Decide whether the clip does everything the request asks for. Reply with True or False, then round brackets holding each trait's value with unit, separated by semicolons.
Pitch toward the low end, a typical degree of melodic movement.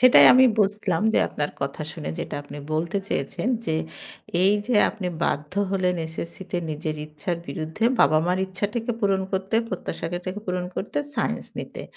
False (180 Hz; 4.1 semitones)